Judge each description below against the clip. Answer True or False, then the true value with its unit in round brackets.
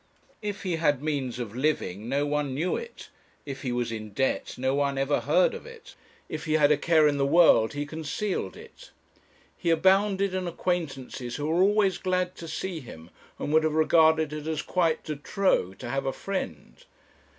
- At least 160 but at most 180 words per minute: False (195 wpm)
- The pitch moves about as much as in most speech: True (4.9 semitones)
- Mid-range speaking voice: True (155 Hz)